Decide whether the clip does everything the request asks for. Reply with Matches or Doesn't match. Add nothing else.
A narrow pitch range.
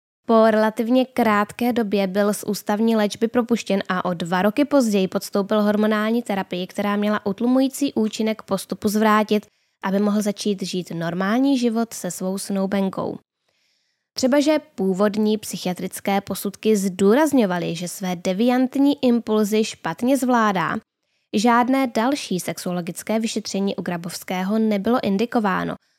Doesn't match